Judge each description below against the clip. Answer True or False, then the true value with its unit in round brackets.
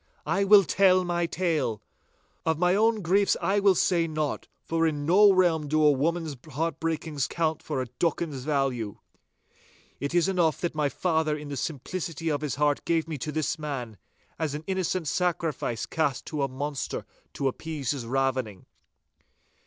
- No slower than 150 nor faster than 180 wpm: True (175 wpm)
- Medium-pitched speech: True (155 Hz)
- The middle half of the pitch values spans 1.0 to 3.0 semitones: False (3.5 semitones)